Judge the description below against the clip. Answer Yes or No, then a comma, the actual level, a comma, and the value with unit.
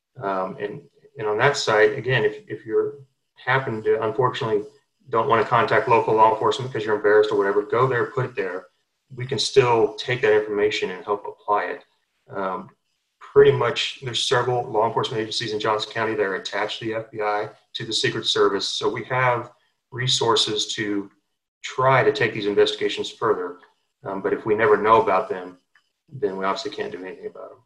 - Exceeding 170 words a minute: Yes, average, 190 wpm